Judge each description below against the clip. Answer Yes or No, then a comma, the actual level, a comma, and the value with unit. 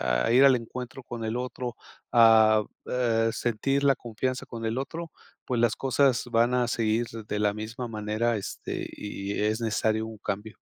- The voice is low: Yes, low, 115 Hz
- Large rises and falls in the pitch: No, narrow, 2.4 semitones